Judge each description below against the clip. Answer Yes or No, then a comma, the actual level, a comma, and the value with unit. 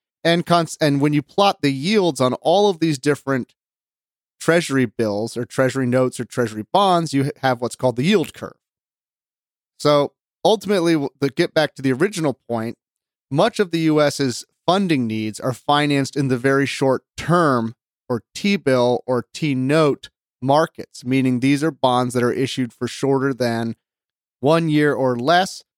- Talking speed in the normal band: Yes, average, 170 wpm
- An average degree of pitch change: Yes, average, 4.2 semitones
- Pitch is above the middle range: No, medium, 140 Hz